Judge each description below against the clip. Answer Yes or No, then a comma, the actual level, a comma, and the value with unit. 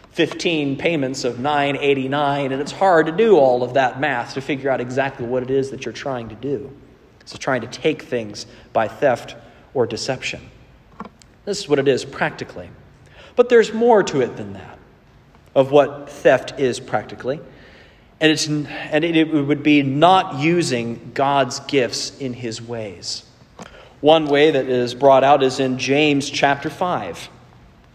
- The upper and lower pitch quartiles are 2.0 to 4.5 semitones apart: Yes, average, 2.8 semitones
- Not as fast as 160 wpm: No, average, 165 wpm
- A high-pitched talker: No, medium, 140 Hz